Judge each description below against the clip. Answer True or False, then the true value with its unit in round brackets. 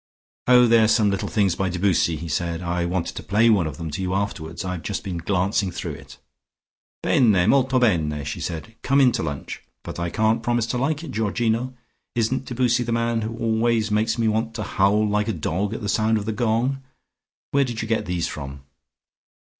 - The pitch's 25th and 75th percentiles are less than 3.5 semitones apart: False (4.6 semitones)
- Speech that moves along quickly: True (210 wpm)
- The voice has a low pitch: True (110 Hz)